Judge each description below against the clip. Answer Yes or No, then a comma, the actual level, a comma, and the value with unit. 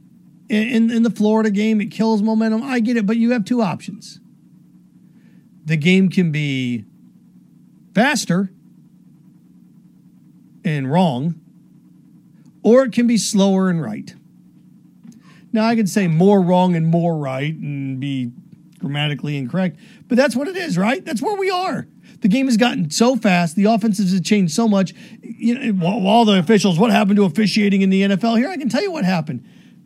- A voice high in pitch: Yes, high, 200 Hz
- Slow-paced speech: No, average, 170 wpm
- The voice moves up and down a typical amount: Yes, average, 4.0 semitones